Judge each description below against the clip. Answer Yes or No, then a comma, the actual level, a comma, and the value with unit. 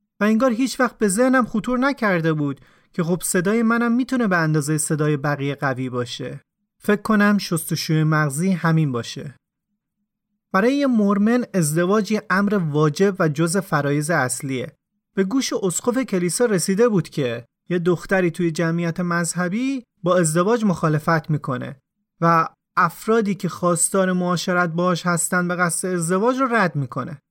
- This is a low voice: No, medium, 180 Hz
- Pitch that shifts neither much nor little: Yes, average, 4.4 semitones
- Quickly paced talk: No, average, 145 wpm